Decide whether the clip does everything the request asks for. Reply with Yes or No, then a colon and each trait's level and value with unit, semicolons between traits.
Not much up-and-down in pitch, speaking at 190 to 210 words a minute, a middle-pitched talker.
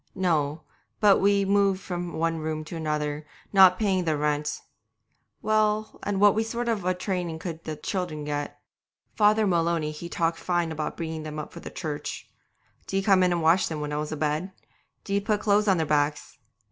No: average, 4.3 semitones; average, 195 wpm; medium, 170 Hz